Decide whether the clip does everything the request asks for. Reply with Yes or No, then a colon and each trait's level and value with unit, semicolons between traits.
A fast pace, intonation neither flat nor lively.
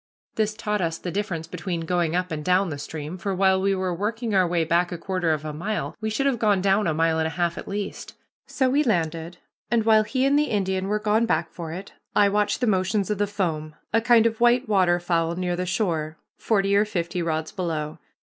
Yes: fast, 230 wpm; average, 4.0 semitones